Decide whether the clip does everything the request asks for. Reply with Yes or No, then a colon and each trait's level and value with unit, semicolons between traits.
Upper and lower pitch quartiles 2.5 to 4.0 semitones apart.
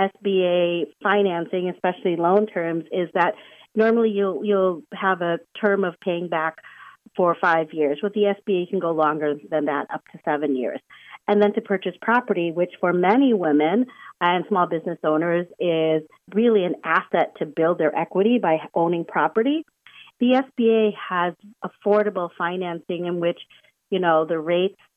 Yes: average, 3.5 semitones